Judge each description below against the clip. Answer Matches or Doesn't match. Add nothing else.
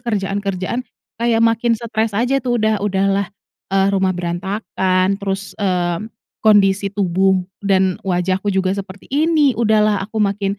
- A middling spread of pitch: Doesn't match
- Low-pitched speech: Doesn't match